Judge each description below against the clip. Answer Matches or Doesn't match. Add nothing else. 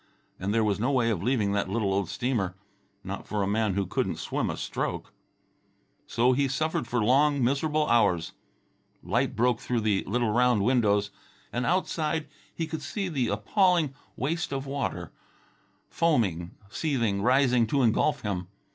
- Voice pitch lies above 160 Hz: Doesn't match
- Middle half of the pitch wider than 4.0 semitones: Matches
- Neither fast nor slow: Matches